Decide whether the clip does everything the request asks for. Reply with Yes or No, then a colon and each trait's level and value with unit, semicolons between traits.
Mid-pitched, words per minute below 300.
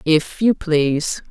Yes: medium, 165 Hz; average, 140 wpm